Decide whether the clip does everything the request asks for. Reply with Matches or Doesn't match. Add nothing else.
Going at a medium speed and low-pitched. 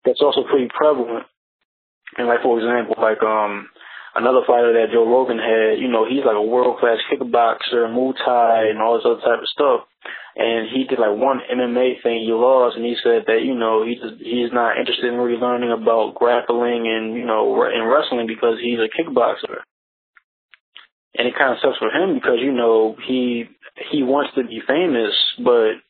Matches